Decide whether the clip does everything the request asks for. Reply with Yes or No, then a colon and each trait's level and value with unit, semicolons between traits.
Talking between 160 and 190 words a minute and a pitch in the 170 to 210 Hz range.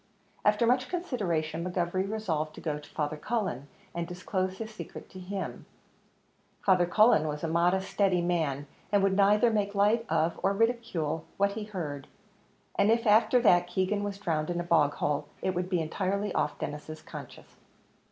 Yes: average, 170 wpm; medium, 185 Hz